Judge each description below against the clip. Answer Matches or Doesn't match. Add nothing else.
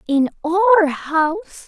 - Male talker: Doesn't match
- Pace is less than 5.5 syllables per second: Matches